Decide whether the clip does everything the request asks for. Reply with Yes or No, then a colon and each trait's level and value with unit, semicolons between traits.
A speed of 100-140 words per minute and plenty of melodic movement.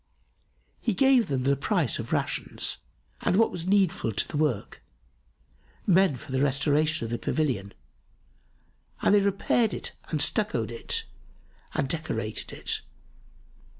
Yes: slow, 135 wpm; wide, 7.3 semitones